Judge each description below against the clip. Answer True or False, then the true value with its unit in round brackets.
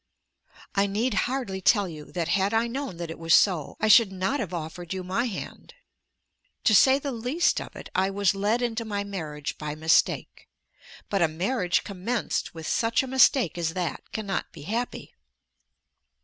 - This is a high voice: True (200 Hz)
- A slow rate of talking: False (175 wpm)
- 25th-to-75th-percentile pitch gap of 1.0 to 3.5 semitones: False (5.1 semitones)